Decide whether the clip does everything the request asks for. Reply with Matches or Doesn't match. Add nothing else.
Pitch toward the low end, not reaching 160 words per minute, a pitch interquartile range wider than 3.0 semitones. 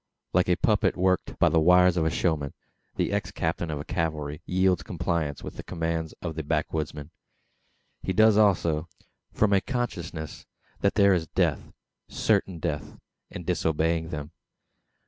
Doesn't match